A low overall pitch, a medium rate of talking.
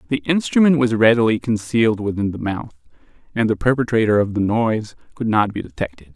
Yes: low, 110 Hz; average, 175 wpm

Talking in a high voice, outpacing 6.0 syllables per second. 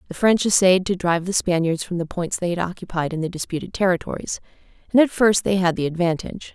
No: medium, 180 Hz; 6.3 syllables/s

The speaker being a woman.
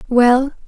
Yes: female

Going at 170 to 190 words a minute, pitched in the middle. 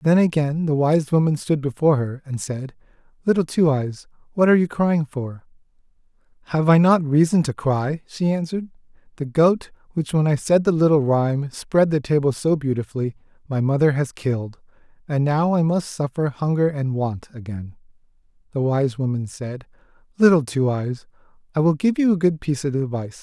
Yes: average, 180 wpm; medium, 145 Hz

